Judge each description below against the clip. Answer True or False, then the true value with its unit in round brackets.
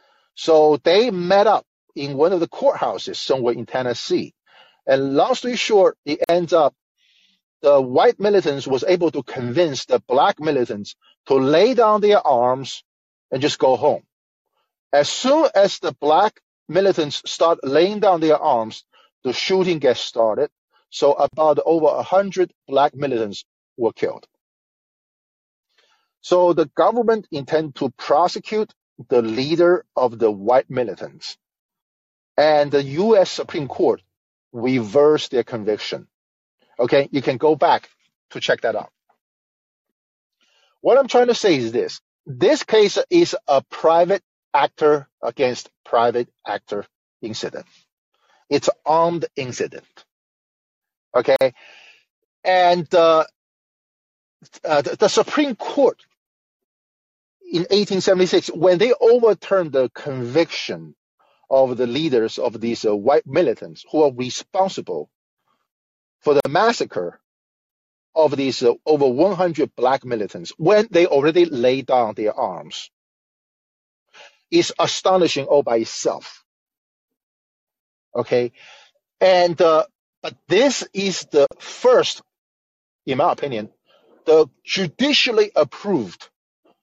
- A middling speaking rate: False (120 wpm)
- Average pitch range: False (7.1 semitones)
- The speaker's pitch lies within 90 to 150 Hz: False (165 Hz)